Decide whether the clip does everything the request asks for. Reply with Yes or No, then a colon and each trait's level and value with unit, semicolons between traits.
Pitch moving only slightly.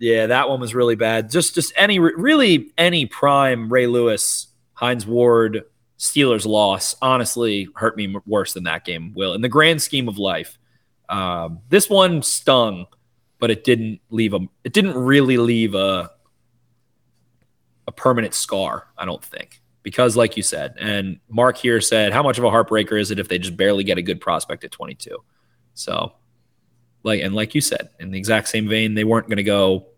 No: average, 3.5 semitones